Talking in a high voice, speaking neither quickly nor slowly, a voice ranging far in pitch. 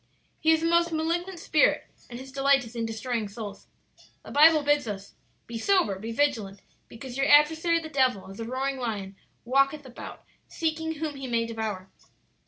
Yes: very high, 270 Hz; average, 180 wpm; wide, 5.7 semitones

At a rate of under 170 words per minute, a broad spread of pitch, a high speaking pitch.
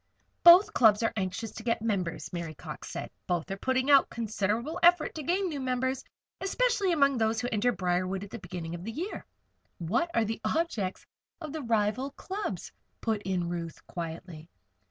No: average, 175 wpm; wide, 7.2 semitones; high, 225 Hz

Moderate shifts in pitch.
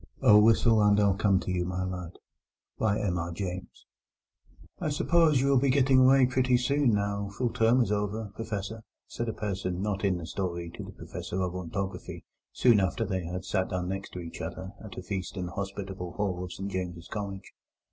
Yes: average, 3.5 semitones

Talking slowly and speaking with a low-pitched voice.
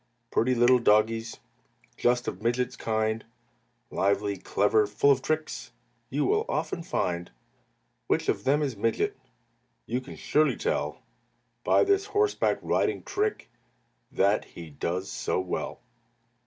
Yes: slow, 130 wpm; low, 120 Hz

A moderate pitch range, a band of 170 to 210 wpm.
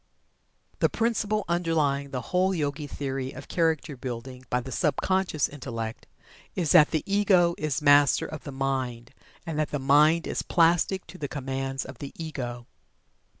No: average, 3.9 semitones; average, 160 wpm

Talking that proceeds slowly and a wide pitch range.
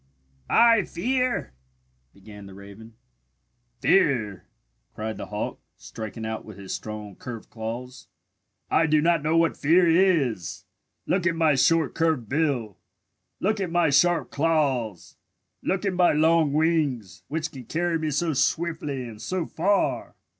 No: average, 145 wpm; wide, 7.1 semitones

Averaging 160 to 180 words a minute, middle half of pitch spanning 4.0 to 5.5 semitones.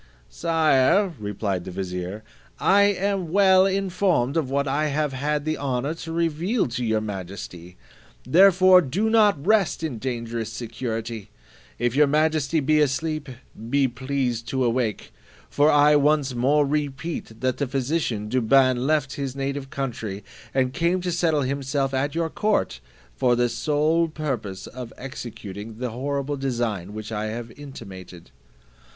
No: average, 145 wpm; average, 5.0 semitones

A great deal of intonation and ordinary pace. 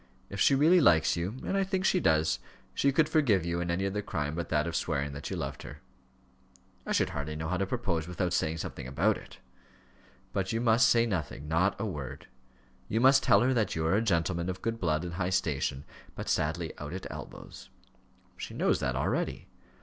No: wide, 6.1 semitones; fast, 210 wpm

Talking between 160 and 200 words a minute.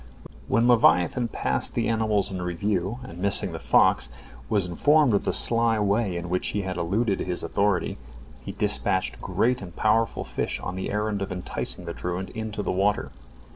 Yes: average, 175 wpm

